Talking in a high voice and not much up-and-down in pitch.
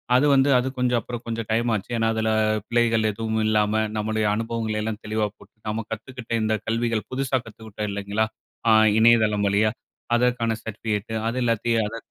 No: low, 110 Hz; narrow, 1.4 semitones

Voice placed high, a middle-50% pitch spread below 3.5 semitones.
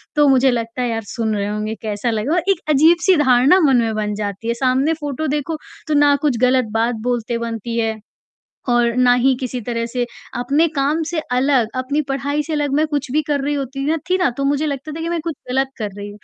No: very high, 260 Hz; average, 4.0 semitones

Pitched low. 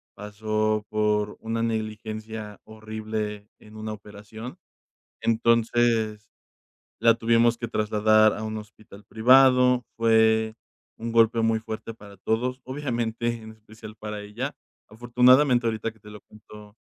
Yes: low, 110 Hz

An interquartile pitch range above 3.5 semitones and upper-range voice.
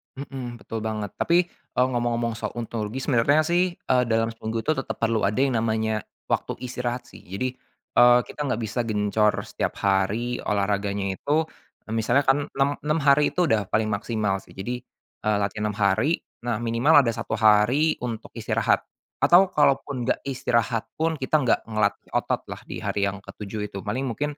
No: average, 4.0 semitones; low, 115 Hz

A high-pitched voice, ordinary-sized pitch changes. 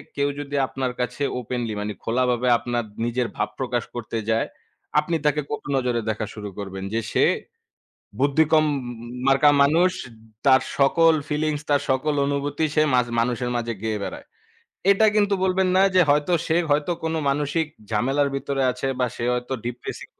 No: low, 135 Hz; average, 3.7 semitones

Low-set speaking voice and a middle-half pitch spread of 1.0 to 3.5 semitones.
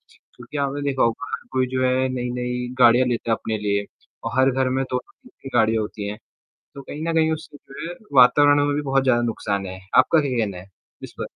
Yes: low, 130 Hz; average, 3.2 semitones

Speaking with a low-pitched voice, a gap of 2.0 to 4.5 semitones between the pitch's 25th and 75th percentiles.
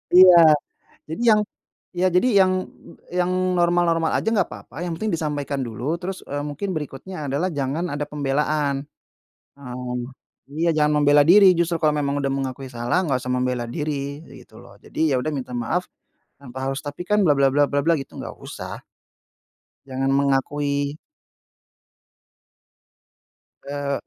No: medium, 145 Hz; average, 3.6 semitones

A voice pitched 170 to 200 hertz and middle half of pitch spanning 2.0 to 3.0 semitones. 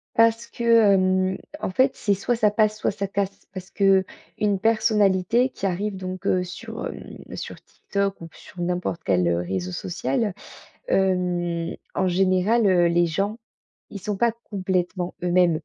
Yes: high, 190 Hz; narrow, 2.6 semitones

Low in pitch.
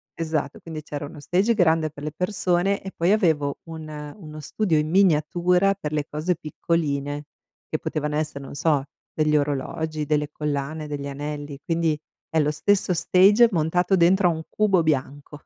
No: medium, 155 Hz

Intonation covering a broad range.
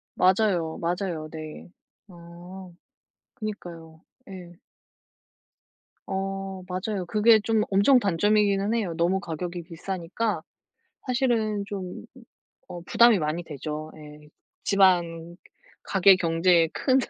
No: average, 3.3 semitones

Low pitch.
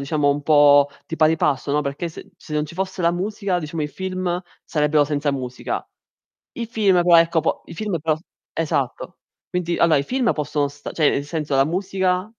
No: medium, 160 Hz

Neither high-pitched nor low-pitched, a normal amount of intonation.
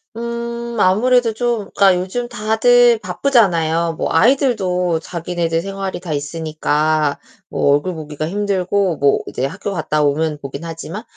No: medium, 180 Hz; wide, 6.0 semitones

